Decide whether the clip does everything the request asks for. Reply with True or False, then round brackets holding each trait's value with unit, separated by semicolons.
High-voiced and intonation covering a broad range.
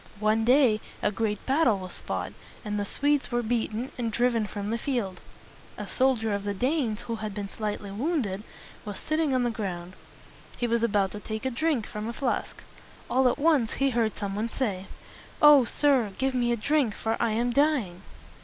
False (230 Hz; 3.9 semitones)